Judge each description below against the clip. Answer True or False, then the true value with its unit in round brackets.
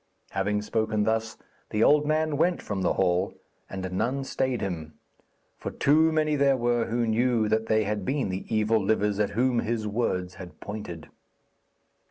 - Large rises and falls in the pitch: False (4.3 semitones)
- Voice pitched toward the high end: False (110 Hz)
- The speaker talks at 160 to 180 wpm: True (170 wpm)